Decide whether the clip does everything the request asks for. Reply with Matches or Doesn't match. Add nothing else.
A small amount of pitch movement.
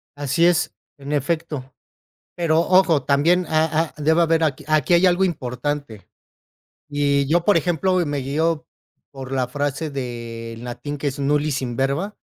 Doesn't match